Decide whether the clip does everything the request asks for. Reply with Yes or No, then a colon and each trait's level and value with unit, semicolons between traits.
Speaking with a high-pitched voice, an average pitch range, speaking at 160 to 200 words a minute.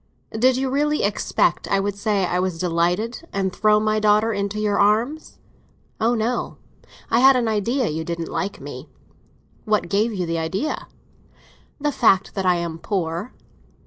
Yes: high, 210 Hz; average, 4.0 semitones; average, 165 wpm